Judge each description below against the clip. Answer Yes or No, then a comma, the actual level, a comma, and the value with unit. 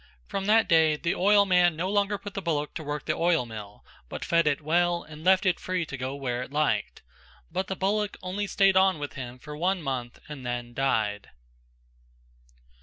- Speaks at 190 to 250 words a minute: Yes, average, 195 wpm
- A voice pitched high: No, medium, 165 Hz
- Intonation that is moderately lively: No, wide, 5.7 semitones